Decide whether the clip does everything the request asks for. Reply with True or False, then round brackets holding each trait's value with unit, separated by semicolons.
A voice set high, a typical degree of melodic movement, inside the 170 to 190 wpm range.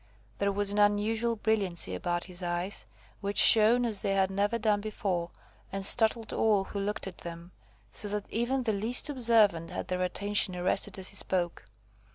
True (205 Hz; 3.0 semitones; 180 wpm)